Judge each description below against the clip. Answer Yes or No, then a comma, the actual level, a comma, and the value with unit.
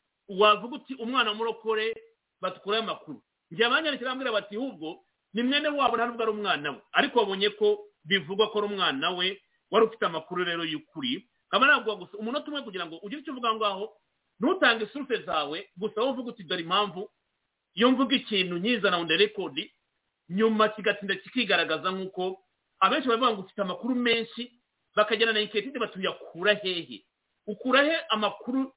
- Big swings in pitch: No, average, 4.1 semitones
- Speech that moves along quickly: No, average, 150 wpm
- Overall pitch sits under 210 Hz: No, high, 215 Hz